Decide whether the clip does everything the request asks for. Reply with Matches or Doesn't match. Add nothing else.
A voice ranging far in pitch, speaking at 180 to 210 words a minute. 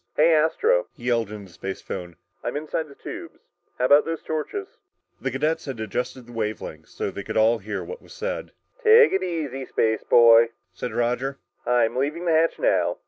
Matches